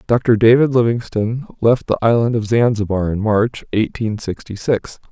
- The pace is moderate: Yes, average, 155 wpm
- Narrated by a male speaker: Yes, male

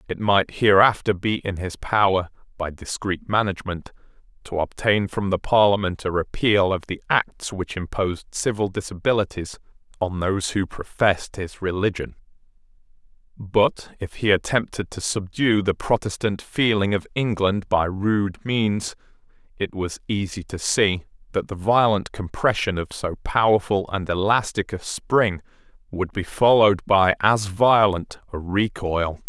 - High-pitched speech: No, low, 100 Hz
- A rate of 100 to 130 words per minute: No, average, 140 wpm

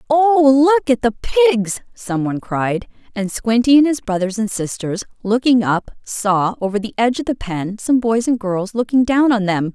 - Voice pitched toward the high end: Yes, high, 230 Hz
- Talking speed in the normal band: Yes, average, 190 wpm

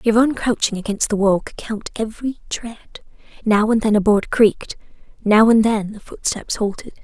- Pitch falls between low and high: No, high, 215 Hz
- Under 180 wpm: Yes, average, 160 wpm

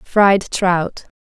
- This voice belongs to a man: No, female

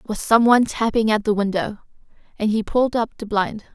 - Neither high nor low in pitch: No, high, 220 Hz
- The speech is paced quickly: Yes, fast, 210 wpm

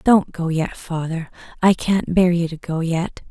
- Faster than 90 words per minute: Yes, average, 200 wpm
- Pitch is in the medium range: Yes, medium, 170 Hz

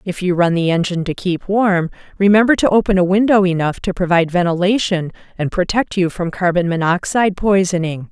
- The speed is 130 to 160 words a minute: No, average, 180 wpm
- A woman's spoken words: Yes, female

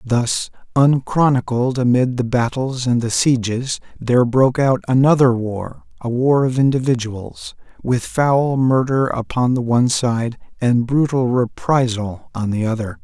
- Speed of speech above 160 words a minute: No, average, 140 wpm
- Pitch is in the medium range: No, low, 125 Hz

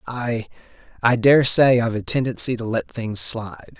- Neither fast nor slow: Yes, average, 160 wpm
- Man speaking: Yes, male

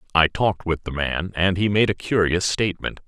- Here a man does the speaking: Yes, male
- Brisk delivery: Yes, fast, 215 wpm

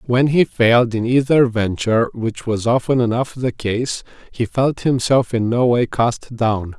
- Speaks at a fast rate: No, average, 160 wpm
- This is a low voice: Yes, low, 120 Hz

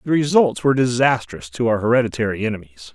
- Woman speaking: No, male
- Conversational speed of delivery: Yes, average, 165 wpm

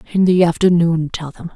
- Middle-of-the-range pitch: Yes, medium, 170 Hz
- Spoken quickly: No, average, 195 wpm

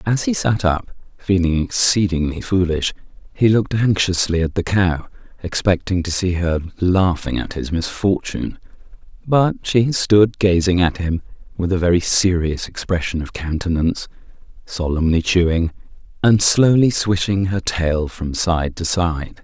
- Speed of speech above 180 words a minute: No, average, 140 wpm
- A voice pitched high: No, very low, 90 Hz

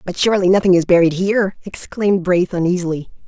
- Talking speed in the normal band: Yes, average, 165 wpm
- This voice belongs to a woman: Yes, female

